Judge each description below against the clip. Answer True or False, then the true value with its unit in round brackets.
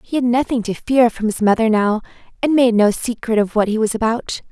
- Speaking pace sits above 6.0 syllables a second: False (5.6 syllables/s)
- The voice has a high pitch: True (230 Hz)